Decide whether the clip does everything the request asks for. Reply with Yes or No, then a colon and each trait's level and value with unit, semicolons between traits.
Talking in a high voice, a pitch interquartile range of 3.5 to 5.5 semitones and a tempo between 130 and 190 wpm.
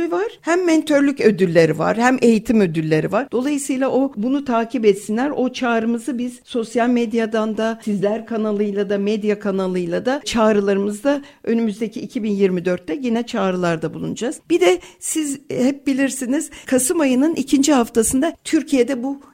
Yes: high, 235 Hz; average, 4.7 semitones; average, 135 wpm